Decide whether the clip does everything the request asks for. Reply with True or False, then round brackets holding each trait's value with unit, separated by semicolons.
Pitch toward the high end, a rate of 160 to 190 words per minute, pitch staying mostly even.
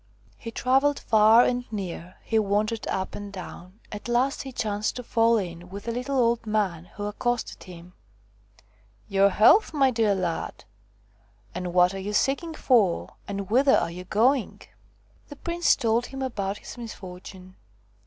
False (210 Hz; 170 wpm; 4.6 semitones)